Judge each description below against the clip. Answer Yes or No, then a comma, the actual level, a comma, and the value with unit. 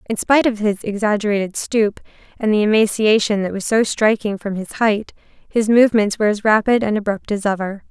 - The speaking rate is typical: Yes, average, 190 wpm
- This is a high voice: Yes, high, 210 Hz